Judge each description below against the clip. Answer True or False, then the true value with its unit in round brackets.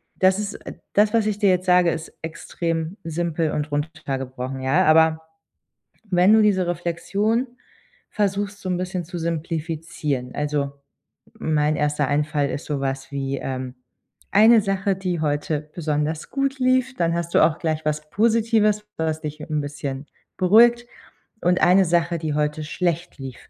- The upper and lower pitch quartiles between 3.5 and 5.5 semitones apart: True (4.4 semitones)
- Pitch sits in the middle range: True (165 Hz)